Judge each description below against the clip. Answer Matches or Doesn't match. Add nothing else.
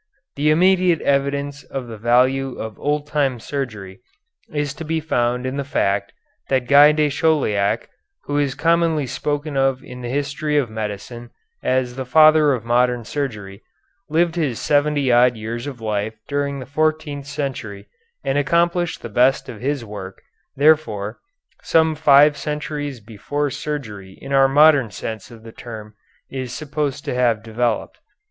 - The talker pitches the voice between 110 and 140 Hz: Matches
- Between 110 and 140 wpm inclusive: Doesn't match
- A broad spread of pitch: Doesn't match